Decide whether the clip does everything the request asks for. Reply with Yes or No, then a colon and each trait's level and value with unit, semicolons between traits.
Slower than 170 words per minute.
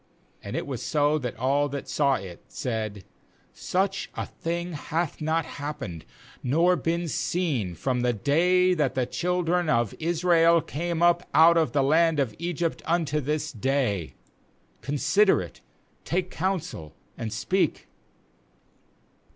Yes: slow, 135 wpm